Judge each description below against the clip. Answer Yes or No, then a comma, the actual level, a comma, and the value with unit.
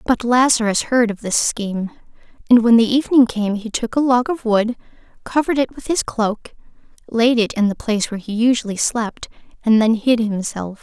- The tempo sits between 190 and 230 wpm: Yes, average, 195 wpm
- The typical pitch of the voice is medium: No, high, 230 Hz